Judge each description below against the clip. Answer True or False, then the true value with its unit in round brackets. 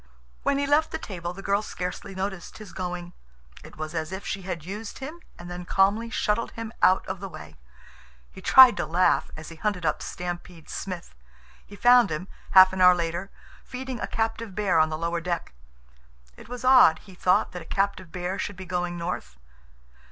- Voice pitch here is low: False (185 Hz)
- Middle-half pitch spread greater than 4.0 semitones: False (3.3 semitones)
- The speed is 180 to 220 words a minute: True (195 wpm)